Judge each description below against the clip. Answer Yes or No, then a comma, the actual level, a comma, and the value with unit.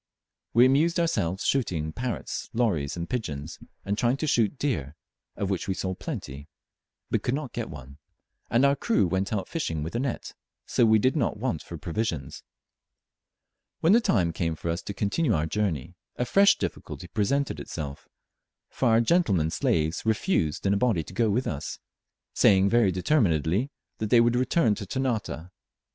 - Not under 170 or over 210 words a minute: Yes, average, 175 wpm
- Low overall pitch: Yes, low, 105 Hz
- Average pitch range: No, wide, 7.1 semitones